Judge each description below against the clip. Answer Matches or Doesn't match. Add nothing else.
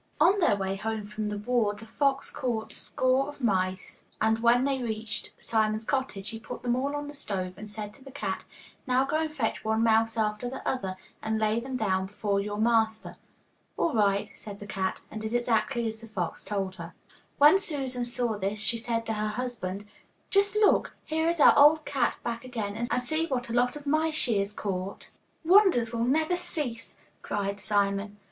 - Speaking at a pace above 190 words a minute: Matches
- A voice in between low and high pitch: Doesn't match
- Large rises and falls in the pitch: Doesn't match